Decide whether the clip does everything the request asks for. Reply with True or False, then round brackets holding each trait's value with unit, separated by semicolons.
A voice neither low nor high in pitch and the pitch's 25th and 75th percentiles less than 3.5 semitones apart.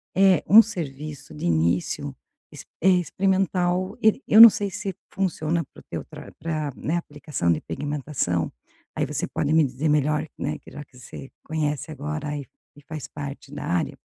False (150 Hz; 4.1 semitones)